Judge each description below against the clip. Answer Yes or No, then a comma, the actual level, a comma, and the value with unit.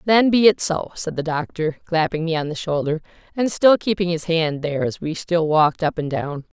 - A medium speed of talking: No, fast, 230 wpm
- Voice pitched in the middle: Yes, medium, 165 Hz